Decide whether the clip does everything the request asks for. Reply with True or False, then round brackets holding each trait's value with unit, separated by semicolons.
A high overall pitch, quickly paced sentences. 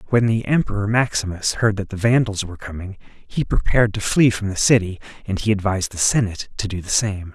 False (105 Hz; 210 wpm)